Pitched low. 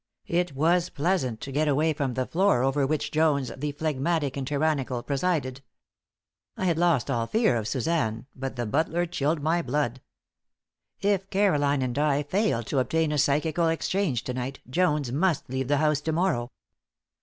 No: medium, 145 Hz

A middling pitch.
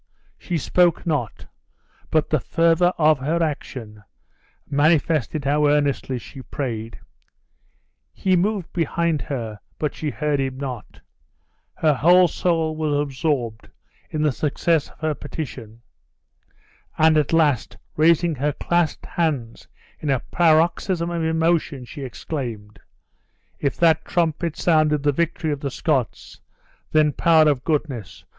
Yes: medium, 150 Hz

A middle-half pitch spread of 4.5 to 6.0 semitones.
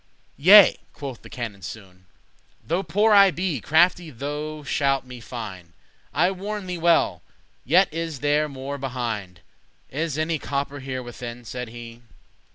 Yes: wide, 5.6 semitones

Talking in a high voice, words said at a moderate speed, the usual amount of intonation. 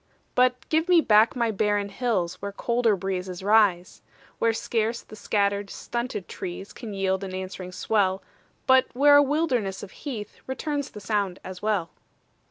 Yes: high, 210 Hz; average, 160 wpm; average, 4.2 semitones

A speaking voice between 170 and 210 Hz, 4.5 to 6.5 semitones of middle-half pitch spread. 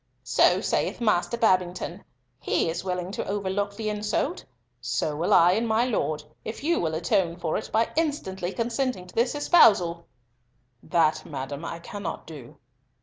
Yes: high, 190 Hz; average, 4.8 semitones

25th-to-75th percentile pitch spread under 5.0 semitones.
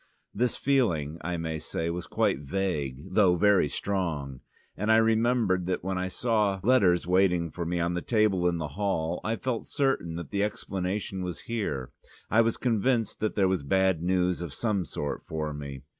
Yes: average, 4.2 semitones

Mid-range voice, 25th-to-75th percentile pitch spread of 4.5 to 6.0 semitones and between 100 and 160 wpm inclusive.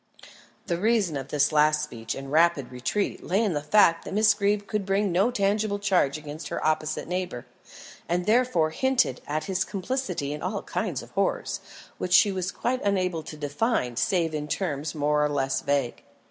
No: medium, 170 Hz; average, 5.3 semitones; average, 185 wpm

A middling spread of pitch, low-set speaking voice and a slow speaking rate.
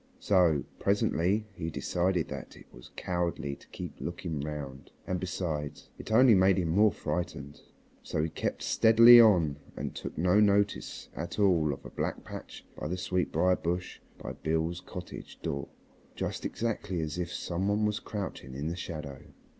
No: average, 4.0 semitones; very low, 90 Hz; average, 165 wpm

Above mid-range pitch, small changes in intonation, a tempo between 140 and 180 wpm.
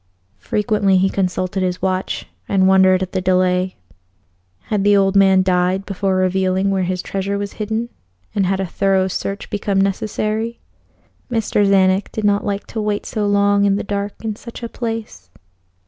Yes: high, 195 Hz; narrow, 1.6 semitones; average, 170 wpm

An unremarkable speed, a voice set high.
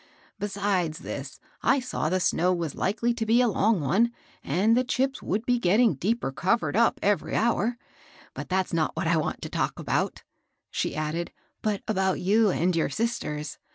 Yes: average, 180 wpm; high, 195 Hz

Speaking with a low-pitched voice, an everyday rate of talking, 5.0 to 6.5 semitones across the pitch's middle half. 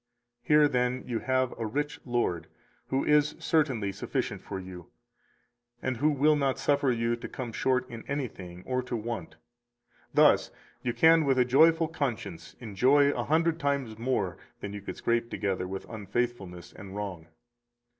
Yes: low, 125 Hz; average, 165 wpm; wide, 5.5 semitones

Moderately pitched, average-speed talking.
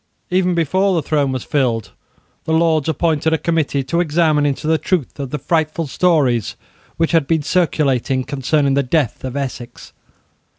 Yes: medium, 150 Hz; average, 165 wpm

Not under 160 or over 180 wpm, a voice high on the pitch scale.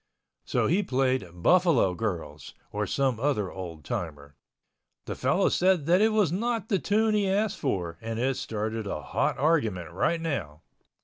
No: average, 165 wpm; low, 130 Hz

